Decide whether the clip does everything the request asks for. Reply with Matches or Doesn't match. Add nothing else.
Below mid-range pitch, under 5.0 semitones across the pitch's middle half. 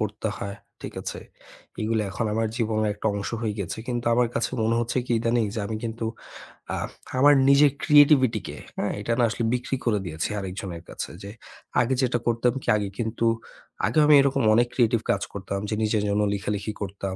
Matches